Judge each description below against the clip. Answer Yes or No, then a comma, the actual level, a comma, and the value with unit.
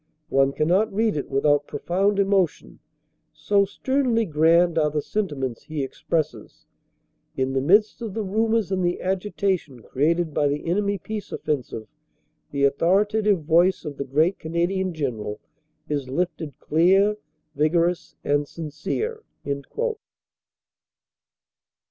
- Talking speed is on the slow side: Yes, slow, 125 wpm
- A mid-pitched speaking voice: Yes, medium, 170 Hz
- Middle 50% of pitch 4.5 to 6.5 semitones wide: Yes, average, 5.3 semitones